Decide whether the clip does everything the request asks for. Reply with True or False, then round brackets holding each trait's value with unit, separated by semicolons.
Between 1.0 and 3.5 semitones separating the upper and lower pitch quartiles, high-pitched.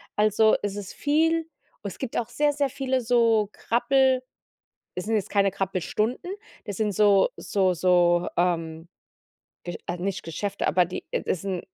False (5.0 semitones; 205 Hz)